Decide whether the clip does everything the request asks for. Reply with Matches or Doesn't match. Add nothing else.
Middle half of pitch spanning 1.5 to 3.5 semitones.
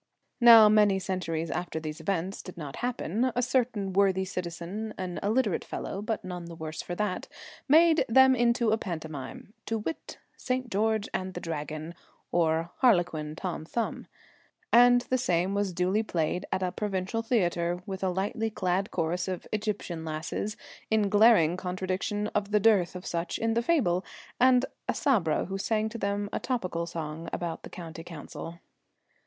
Doesn't match